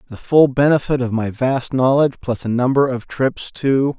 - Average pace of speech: Yes, average, 195 wpm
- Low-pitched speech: Yes, low, 130 Hz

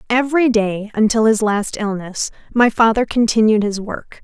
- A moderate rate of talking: Yes, average, 155 wpm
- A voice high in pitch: Yes, high, 220 Hz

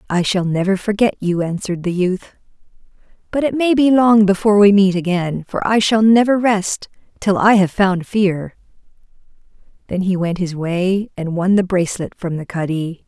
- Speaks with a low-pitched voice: No, high, 190 Hz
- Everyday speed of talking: Yes, average, 180 wpm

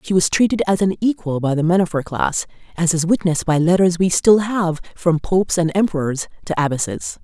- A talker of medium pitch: Yes, medium, 175 Hz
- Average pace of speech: No, fast, 215 wpm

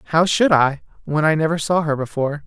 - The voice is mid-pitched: Yes, medium, 155 Hz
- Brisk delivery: Yes, fast, 220 wpm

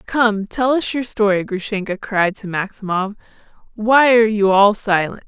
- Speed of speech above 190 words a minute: No, average, 160 wpm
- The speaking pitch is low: No, high, 210 Hz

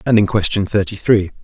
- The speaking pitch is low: Yes, low, 100 Hz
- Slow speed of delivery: No, fast, 210 wpm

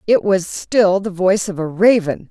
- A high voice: Yes, high, 195 Hz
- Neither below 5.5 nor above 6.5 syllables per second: No, 4.6 syllables/s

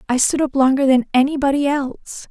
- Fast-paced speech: No, average, 185 wpm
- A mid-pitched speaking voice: No, very high, 270 Hz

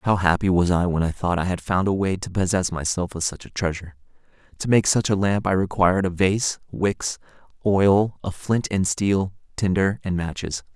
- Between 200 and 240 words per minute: Yes, fast, 205 wpm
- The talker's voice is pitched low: Yes, very low, 95 Hz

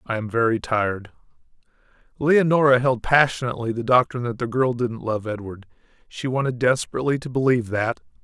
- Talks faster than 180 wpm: No, average, 155 wpm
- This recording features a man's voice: Yes, male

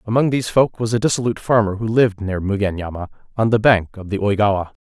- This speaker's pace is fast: Yes, fast, 210 wpm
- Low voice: Yes, low, 105 Hz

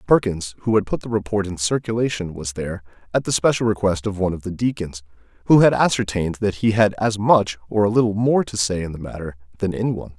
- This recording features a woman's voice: No, male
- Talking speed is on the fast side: Yes, fast, 230 wpm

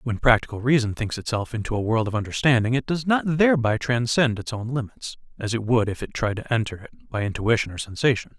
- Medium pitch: No, low, 120 Hz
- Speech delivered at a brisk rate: Yes, fast, 220 wpm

